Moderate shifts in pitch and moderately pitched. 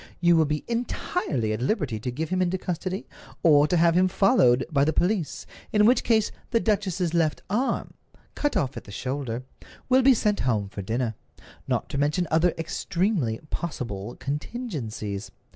No: wide, 7.6 semitones; medium, 160 Hz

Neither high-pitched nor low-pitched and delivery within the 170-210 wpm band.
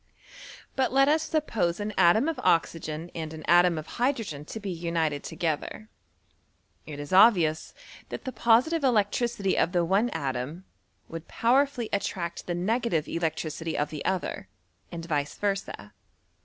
No: medium, 175 Hz; average, 150 wpm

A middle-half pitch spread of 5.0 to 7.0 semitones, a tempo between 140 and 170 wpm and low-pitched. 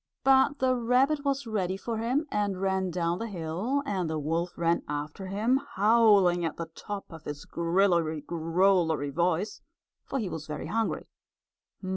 No: wide, 5.4 semitones; average, 160 wpm; high, 190 Hz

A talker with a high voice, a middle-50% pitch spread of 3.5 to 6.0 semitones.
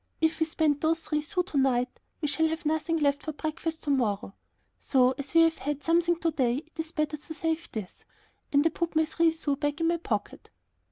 No: very high, 310 Hz; narrow, 2.4 semitones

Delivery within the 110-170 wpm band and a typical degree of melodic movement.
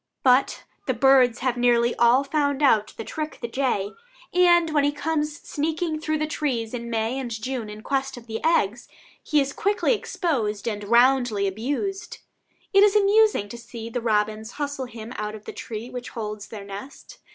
No: average, 180 wpm; average, 5.0 semitones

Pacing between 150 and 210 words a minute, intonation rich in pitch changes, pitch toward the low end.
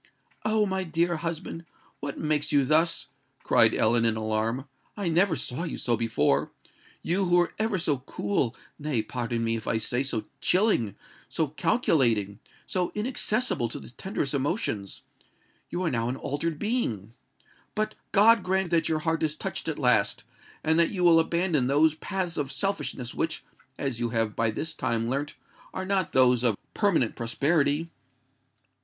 No: average, 155 wpm; wide, 6.6 semitones; medium, 150 Hz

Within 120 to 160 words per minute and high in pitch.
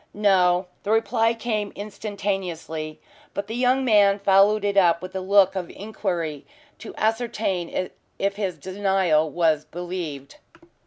Yes: slow, 135 wpm; high, 195 Hz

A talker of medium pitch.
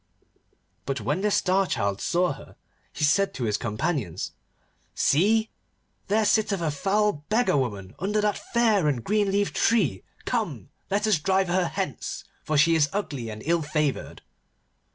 Yes: medium, 170 Hz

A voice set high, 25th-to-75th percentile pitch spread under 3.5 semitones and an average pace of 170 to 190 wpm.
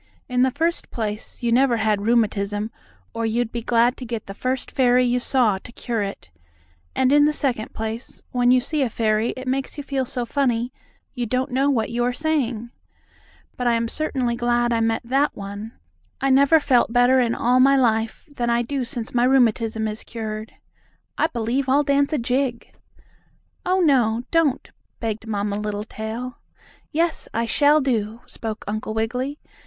Yes: high, 240 Hz; average, 2.9 semitones; average, 180 wpm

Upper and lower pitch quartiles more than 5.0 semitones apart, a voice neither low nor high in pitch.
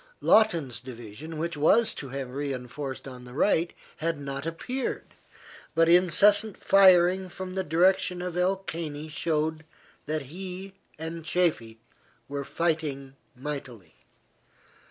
No: average, 4.7 semitones; medium, 160 Hz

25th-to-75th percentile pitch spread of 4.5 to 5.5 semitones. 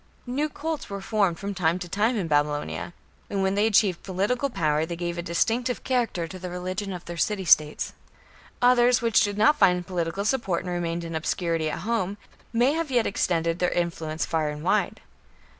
Yes: average, 4.8 semitones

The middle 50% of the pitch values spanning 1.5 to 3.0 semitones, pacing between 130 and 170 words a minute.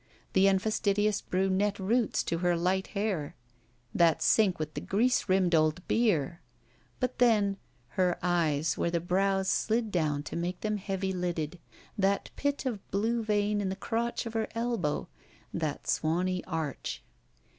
No: average, 3.6 semitones; average, 150 wpm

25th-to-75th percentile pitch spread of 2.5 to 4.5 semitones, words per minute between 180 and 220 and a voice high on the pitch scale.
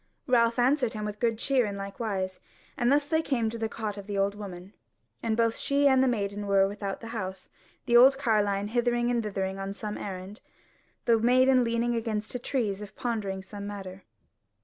Yes: average, 3.3 semitones; average, 200 wpm; high, 220 Hz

